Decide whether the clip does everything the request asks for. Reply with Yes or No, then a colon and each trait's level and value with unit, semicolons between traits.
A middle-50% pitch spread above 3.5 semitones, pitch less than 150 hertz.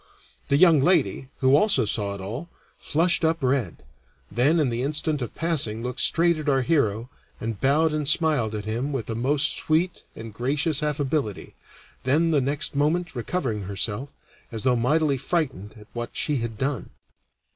Yes: average, 5.0 semitones; low, 135 Hz